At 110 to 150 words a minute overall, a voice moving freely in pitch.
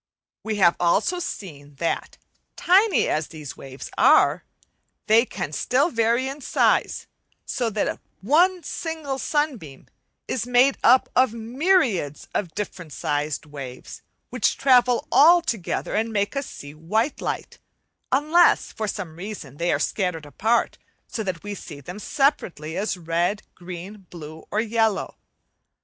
Yes: average, 140 wpm; wide, 7.6 semitones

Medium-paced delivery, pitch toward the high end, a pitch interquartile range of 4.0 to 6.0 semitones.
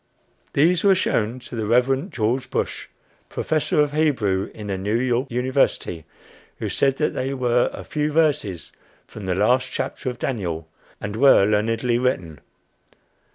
No: average, 155 wpm; low, 125 Hz; average, 4.6 semitones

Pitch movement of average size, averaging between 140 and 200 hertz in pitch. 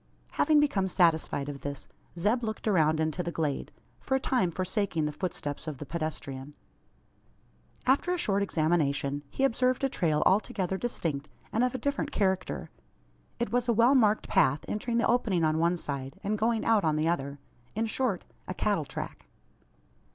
No: wide, 6.9 semitones; medium, 185 Hz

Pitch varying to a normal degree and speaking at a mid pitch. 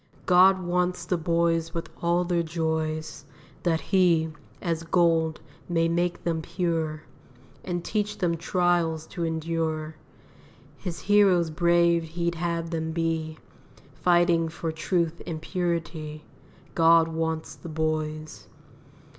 No: narrow, 1.4 semitones; medium, 165 Hz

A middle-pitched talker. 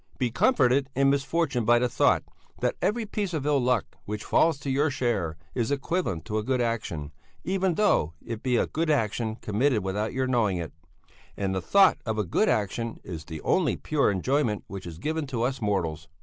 No: low, 120 Hz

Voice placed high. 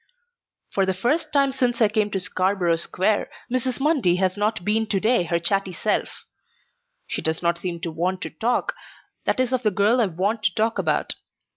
Yes: high, 205 Hz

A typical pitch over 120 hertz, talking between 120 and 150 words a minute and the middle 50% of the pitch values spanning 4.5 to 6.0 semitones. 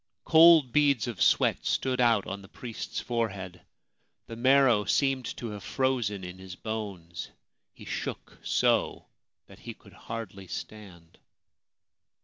No: low, 110 Hz; slow, 135 wpm; average, 4.9 semitones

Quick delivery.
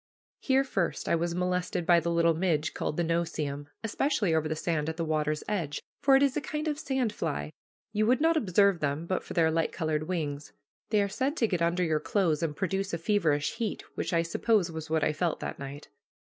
Yes: fast, 230 wpm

